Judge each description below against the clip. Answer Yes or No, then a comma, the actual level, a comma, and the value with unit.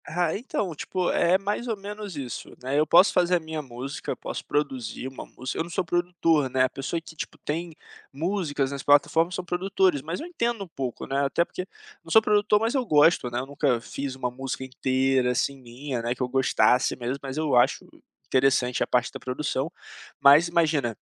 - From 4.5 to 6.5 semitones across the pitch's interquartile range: Yes, average, 5.1 semitones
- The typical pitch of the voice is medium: Yes, medium, 145 Hz